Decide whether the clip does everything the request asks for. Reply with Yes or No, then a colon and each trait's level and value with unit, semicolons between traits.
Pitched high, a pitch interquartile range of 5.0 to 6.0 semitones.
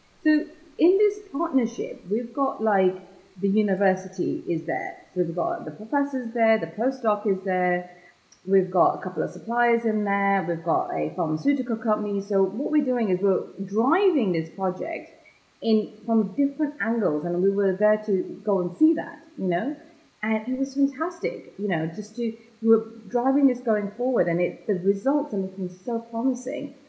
Yes: high, 215 Hz; wide, 5.5 semitones